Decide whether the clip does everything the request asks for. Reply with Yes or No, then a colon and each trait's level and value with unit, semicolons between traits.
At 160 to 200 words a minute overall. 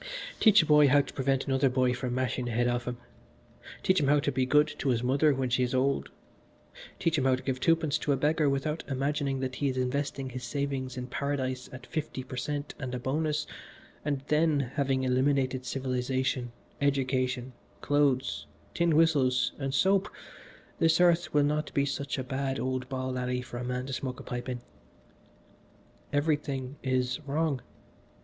Yes: average, 185 wpm